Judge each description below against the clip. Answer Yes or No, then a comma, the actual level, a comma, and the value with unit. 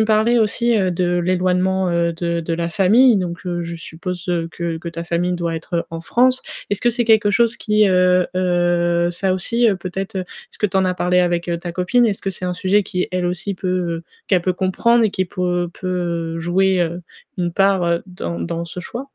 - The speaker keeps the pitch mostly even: Yes, narrow, 2.2 semitones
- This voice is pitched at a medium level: Yes, medium, 180 Hz